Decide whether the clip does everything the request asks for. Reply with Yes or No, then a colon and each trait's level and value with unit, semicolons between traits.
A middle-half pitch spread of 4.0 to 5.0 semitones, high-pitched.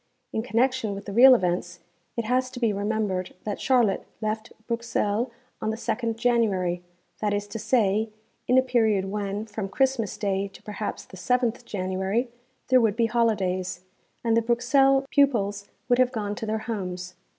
No: average, 3.3 semitones; high, 220 Hz